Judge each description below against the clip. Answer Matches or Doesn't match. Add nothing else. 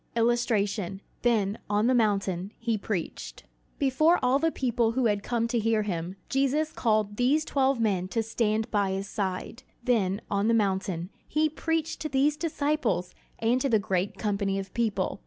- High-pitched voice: Matches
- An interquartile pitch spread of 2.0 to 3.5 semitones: Doesn't match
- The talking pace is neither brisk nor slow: Matches